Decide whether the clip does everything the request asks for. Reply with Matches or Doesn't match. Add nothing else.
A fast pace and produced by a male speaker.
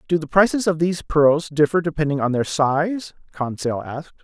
Doesn't match